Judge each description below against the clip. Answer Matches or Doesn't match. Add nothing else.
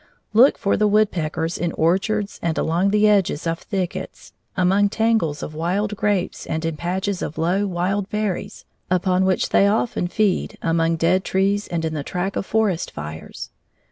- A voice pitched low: Doesn't match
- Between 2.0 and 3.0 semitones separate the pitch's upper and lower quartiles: Doesn't match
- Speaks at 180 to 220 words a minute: Doesn't match